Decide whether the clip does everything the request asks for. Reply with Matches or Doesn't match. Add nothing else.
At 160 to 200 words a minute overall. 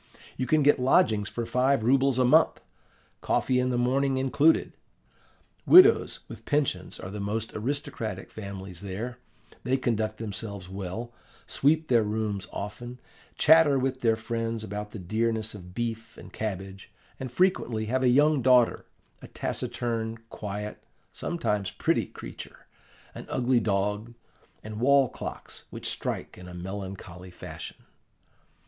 Doesn't match